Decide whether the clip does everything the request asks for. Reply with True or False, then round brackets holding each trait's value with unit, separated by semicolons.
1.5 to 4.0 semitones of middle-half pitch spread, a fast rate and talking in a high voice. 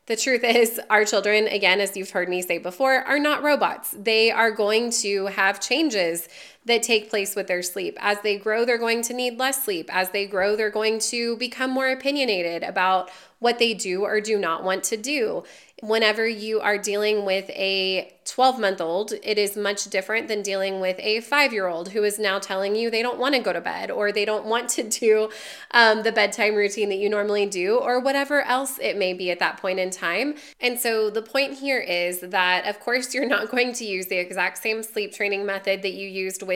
True (3.5 semitones; 225 wpm; 215 Hz)